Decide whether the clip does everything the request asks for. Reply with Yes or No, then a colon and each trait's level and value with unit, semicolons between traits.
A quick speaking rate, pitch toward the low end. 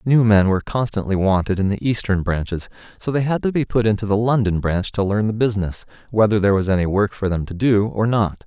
Yes: fast, 240 wpm; low, 105 Hz